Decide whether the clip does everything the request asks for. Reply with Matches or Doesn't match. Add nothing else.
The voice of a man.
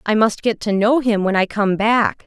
Doesn't match